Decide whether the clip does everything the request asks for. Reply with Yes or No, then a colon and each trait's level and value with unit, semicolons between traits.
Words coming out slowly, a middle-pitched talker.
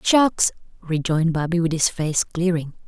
Yes: slow, 125 wpm; medium, 170 Hz